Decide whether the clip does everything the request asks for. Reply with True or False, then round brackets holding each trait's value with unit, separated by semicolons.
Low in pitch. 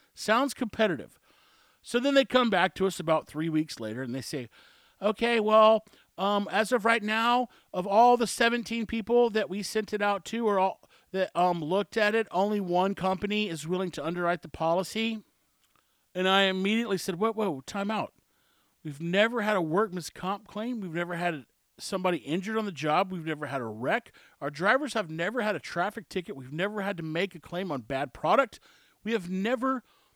False (195 Hz)